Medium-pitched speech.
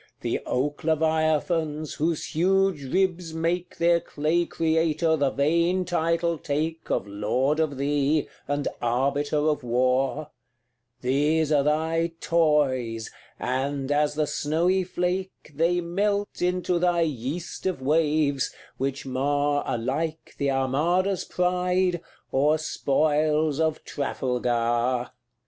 Yes: medium, 155 Hz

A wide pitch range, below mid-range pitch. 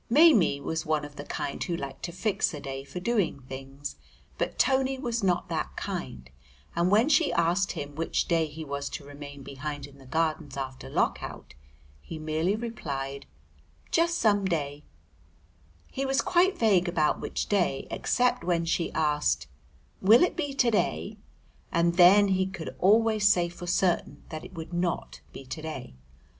No: wide, 6.3 semitones; medium, 170 Hz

